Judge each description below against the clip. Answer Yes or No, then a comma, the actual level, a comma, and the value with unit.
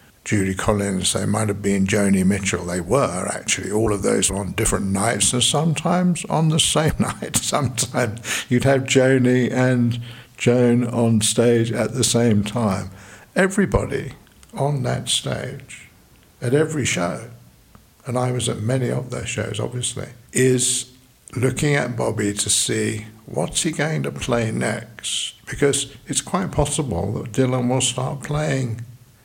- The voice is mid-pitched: No, low, 120 Hz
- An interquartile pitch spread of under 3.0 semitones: No, average, 3.4 semitones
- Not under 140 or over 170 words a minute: Yes, average, 150 wpm